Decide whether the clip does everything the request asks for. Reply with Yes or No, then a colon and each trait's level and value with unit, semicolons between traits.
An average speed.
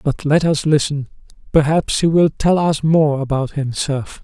Yes: average, 170 wpm